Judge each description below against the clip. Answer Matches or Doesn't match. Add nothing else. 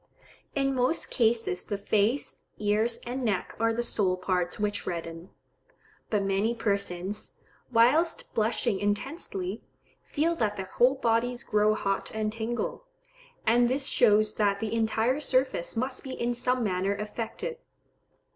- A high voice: Matches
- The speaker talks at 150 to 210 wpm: Doesn't match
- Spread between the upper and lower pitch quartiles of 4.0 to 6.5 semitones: Doesn't match